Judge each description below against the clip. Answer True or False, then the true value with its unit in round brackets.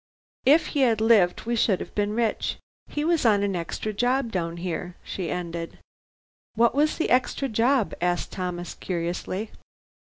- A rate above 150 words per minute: True (160 wpm)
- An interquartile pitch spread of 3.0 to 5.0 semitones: False (5.5 semitones)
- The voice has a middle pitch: False (210 Hz)